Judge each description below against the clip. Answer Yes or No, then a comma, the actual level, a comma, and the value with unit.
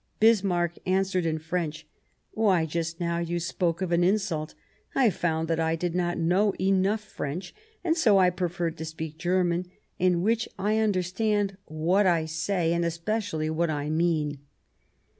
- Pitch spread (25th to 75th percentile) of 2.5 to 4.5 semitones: Yes, average, 3.0 semitones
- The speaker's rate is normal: Yes, average, 160 wpm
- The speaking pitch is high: No, medium, 175 Hz